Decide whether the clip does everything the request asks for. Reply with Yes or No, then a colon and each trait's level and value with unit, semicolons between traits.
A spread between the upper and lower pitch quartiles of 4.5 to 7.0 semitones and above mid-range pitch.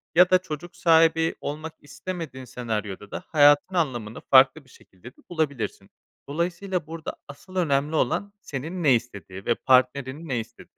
No: average, 4.8 semitones; medium, 145 Hz